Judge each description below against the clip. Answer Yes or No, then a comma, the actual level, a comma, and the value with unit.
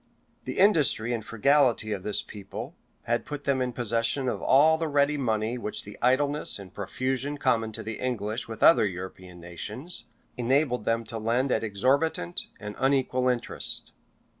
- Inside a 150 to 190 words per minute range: Yes, average, 165 wpm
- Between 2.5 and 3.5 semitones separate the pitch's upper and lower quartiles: No, average, 4.2 semitones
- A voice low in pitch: Yes, low, 120 Hz